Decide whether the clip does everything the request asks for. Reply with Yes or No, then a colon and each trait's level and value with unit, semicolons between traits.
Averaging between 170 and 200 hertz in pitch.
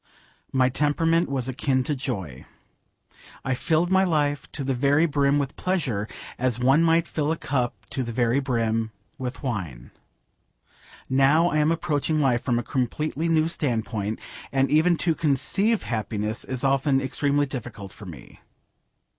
No: low, 135 Hz